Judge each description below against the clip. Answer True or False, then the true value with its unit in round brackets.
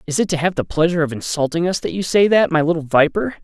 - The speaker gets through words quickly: True (280 wpm)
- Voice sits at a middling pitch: True (165 Hz)